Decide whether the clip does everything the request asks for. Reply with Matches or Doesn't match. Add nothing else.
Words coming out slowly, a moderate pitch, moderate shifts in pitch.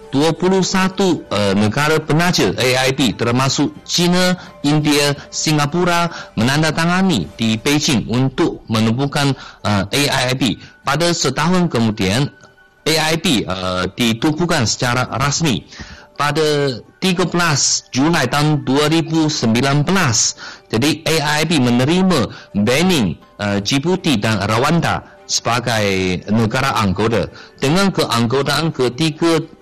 Doesn't match